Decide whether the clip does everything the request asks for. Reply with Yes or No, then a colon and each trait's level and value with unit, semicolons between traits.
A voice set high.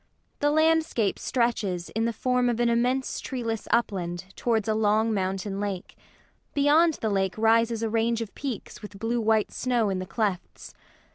Yes: high, 225 Hz